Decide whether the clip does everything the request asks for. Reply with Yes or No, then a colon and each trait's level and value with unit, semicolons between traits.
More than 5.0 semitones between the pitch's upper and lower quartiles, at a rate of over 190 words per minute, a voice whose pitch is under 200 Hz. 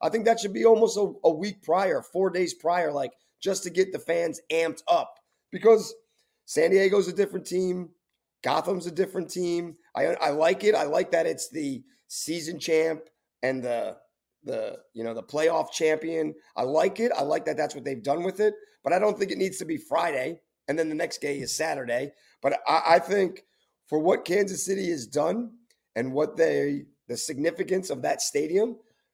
Yes: wide, 5.6 semitones; average, 200 wpm; medium, 185 Hz